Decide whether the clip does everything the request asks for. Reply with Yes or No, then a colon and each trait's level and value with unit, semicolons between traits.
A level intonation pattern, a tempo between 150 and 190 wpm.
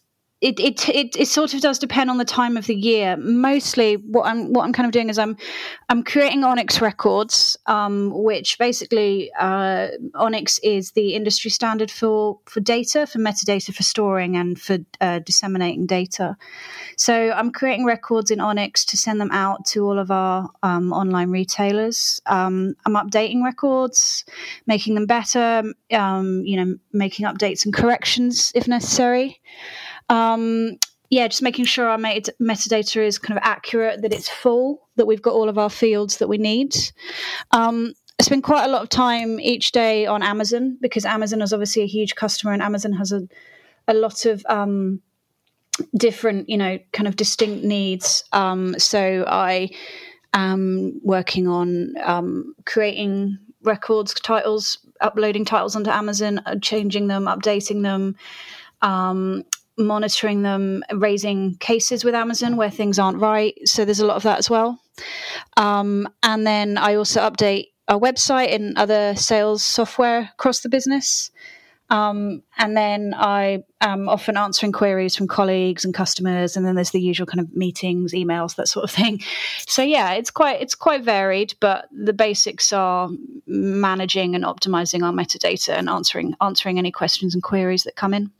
No: average, 3.0 semitones; average, 165 wpm